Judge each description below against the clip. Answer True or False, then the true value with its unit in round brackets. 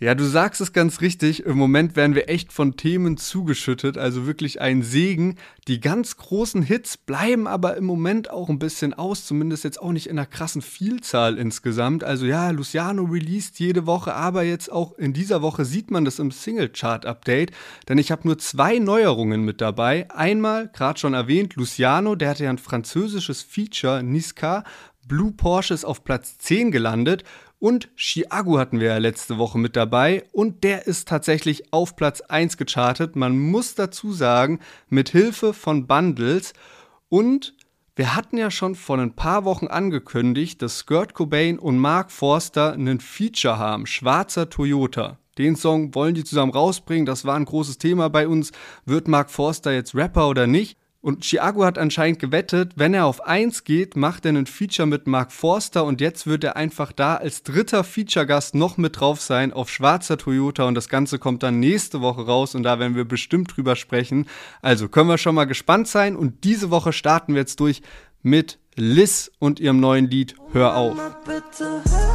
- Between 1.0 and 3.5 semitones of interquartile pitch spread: False (5.1 semitones)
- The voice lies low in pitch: False (155 Hz)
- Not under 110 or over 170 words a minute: False (180 wpm)